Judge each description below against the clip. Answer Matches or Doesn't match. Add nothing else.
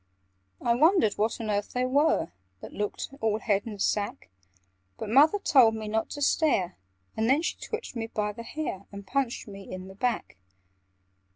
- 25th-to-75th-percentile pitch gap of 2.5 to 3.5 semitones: Doesn't match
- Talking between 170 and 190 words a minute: Matches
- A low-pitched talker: Doesn't match